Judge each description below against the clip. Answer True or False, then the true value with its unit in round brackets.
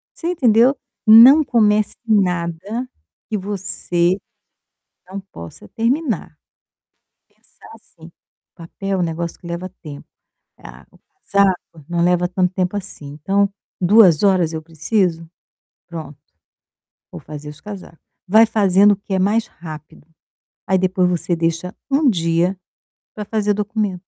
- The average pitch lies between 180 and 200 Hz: True (185 Hz)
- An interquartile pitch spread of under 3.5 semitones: False (3.8 semitones)